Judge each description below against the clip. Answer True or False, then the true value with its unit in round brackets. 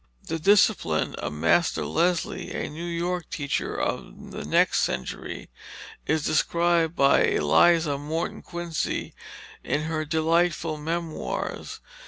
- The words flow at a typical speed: False (115 wpm)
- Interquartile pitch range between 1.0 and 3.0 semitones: True (2.4 semitones)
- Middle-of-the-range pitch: True (160 Hz)